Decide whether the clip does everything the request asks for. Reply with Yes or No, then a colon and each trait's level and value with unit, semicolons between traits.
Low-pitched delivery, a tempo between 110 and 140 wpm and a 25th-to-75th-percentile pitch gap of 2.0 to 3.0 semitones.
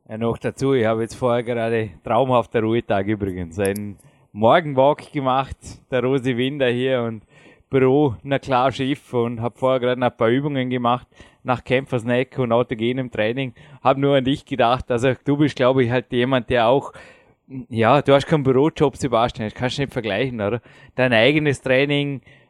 No: low, 125 Hz; average, 175 wpm; narrow, 2.6 semitones